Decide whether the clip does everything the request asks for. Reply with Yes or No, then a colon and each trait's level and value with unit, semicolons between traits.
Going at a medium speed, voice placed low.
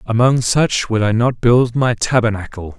Yes: average, 170 wpm; low, 115 Hz